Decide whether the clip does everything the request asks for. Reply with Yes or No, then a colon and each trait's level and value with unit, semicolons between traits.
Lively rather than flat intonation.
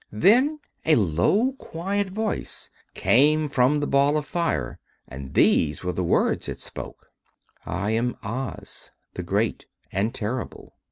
Yes: wide, 8.6 semitones